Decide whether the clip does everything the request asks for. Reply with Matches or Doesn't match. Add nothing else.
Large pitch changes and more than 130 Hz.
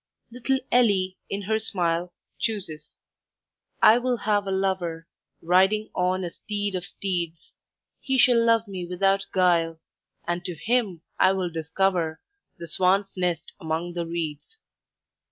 Doesn't match